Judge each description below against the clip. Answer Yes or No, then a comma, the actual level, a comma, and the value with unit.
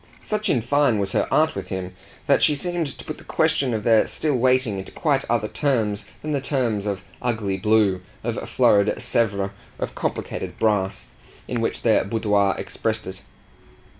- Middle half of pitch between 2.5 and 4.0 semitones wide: No, average, 4.8 semitones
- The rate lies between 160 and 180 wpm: Yes, average, 175 wpm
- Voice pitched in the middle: No, low, 110 Hz